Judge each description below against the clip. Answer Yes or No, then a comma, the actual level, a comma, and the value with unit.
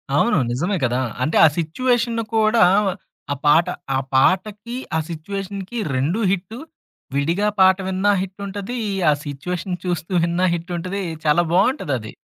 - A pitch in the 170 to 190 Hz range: Yes, medium, 185 Hz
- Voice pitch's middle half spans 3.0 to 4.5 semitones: Yes, average, 3.8 semitones